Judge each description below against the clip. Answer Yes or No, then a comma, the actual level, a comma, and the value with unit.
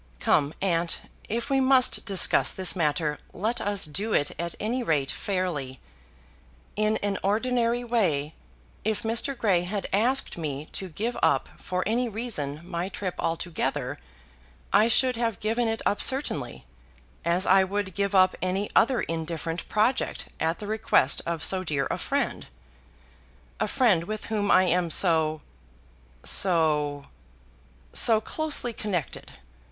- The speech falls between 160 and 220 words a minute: No, average, 140 wpm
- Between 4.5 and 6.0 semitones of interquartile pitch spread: Yes, average, 5.2 semitones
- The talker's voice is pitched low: No, high, 195 Hz